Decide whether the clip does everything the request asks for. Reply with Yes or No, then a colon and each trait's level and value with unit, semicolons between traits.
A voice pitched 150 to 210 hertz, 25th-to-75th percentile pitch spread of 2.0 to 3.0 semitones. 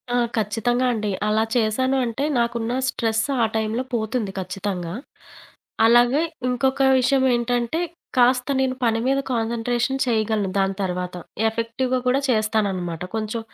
No: high, 230 Hz; narrow, 2.6 semitones